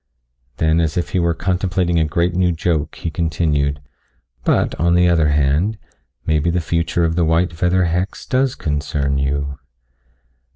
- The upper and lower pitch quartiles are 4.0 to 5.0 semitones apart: No, average, 2.7 semitones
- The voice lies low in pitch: Yes, very low, 85 Hz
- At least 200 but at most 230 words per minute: No, average, 160 wpm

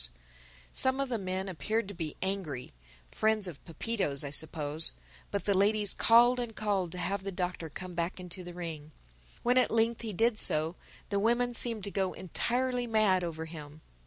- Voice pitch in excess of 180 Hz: Yes, high, 190 Hz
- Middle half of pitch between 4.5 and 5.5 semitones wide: Yes, average, 4.9 semitones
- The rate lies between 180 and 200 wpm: Yes, average, 185 wpm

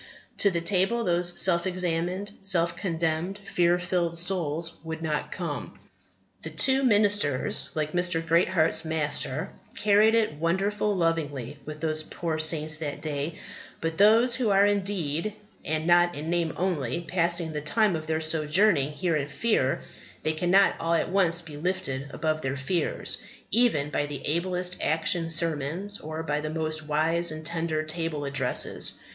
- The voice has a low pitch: No, medium, 165 Hz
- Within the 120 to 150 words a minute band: No, average, 160 wpm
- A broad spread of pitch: No, average, 3.0 semitones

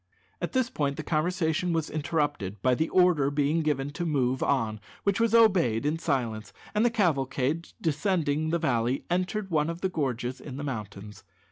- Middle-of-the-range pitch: Yes, medium, 150 Hz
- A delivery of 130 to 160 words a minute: No, average, 175 wpm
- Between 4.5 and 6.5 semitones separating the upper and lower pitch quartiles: Yes, average, 4.8 semitones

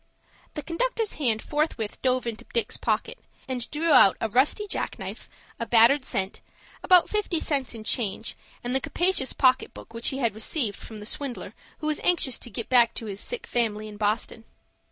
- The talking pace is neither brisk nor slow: Yes, average, 190 wpm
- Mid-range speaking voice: No, very high, 250 Hz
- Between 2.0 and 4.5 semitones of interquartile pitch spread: No, average, 5.2 semitones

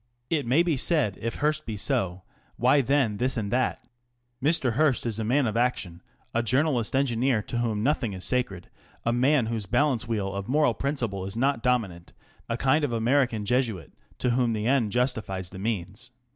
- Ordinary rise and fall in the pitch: Yes, average, 4.1 semitones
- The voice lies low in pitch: Yes, low, 120 Hz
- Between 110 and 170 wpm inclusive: No, average, 190 wpm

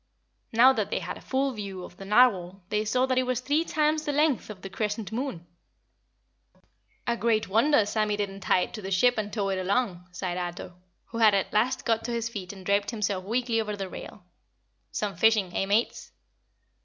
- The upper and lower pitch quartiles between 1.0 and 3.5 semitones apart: No, average, 4.0 semitones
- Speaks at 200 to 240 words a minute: Yes, fast, 205 wpm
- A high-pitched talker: Yes, high, 215 Hz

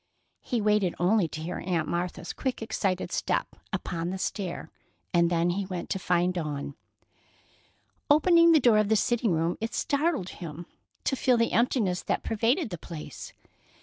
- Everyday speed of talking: Yes, average, 165 wpm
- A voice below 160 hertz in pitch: No, high, 190 Hz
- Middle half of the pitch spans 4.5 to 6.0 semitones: Yes, average, 5.0 semitones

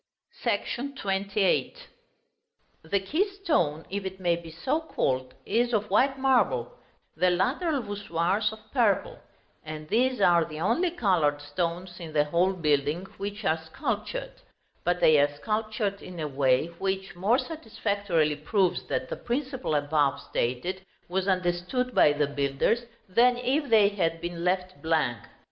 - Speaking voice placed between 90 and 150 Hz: No, high, 190 Hz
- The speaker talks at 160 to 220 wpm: No, average, 145 wpm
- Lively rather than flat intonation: Yes, wide, 6.1 semitones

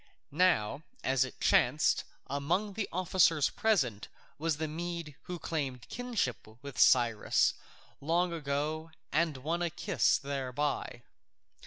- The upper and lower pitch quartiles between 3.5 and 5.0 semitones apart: Yes, average, 4.0 semitones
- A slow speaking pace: Yes, slow, 125 wpm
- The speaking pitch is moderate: Yes, medium, 155 Hz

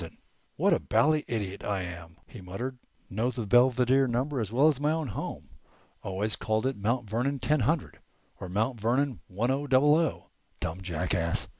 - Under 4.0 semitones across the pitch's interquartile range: No, wide, 5.4 semitones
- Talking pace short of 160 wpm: No, average, 175 wpm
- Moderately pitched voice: No, low, 120 Hz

